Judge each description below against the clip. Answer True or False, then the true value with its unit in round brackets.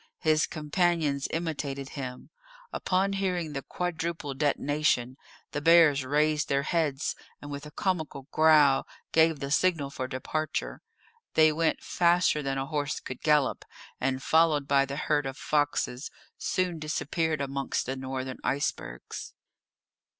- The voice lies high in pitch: False (150 Hz)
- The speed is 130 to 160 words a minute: True (135 wpm)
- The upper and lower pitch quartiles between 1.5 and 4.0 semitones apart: True (2.7 semitones)